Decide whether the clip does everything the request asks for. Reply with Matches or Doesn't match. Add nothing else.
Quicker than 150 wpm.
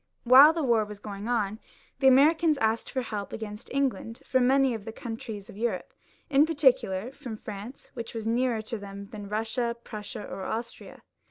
Matches